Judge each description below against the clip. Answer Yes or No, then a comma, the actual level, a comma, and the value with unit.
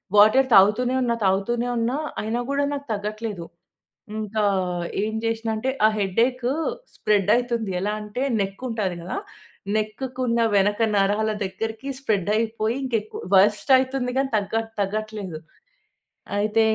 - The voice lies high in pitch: Yes, high, 215 Hz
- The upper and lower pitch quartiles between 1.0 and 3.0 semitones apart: Yes, average, 2.7 semitones